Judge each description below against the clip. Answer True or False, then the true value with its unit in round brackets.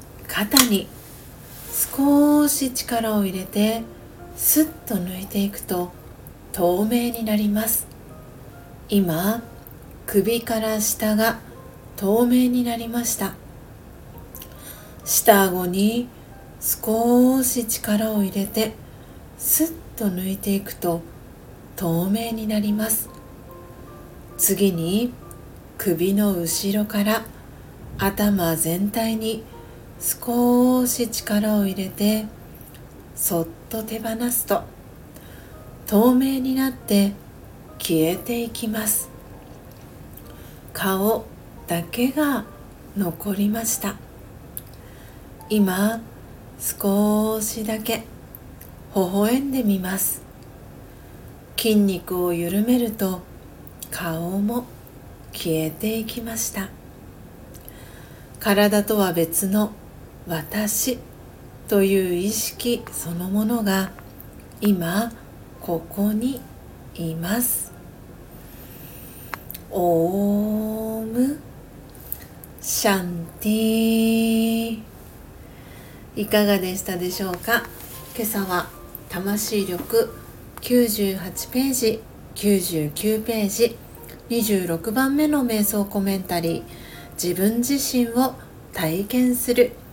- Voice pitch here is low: False (210 Hz)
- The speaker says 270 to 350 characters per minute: False (145 characters per minute)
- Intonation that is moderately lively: True (3.7 semitones)